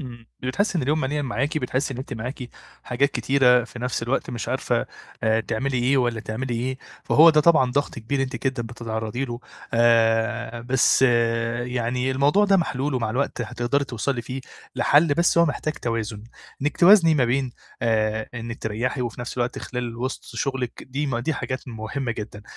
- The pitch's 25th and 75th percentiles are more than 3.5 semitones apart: No, average, 2.9 semitones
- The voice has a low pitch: Yes, low, 125 Hz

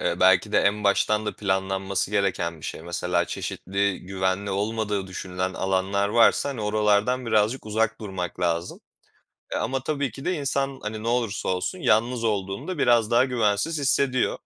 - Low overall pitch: Yes, low, 105 Hz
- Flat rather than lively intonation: No, average, 3.7 semitones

